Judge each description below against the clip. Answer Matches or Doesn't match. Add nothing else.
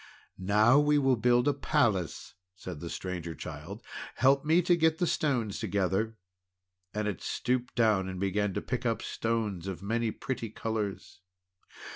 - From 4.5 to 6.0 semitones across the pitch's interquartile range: Matches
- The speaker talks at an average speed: Matches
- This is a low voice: Matches